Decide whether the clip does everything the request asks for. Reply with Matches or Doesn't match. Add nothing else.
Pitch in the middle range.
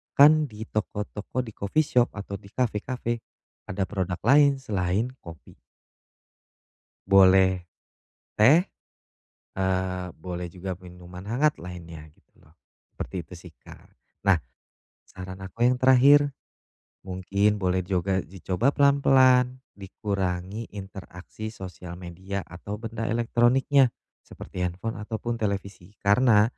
Doesn't match